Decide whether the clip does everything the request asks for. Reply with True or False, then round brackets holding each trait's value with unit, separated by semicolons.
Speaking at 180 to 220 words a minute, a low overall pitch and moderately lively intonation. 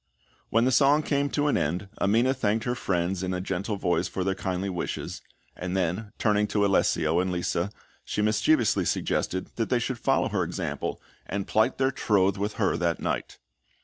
True (185 wpm; 100 Hz; 4.0 semitones)